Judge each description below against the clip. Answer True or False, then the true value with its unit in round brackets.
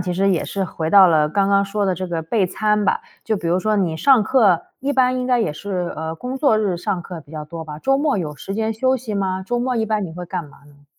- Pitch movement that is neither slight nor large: True (4.7 semitones)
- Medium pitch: False (195 Hz)